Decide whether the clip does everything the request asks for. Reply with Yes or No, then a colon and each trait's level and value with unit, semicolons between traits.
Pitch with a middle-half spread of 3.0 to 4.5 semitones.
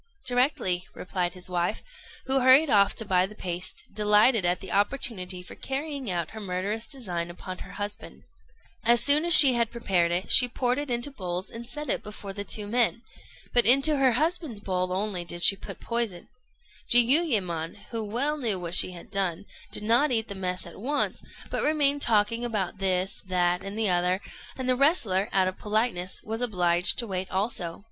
No: average, 5.1 semitones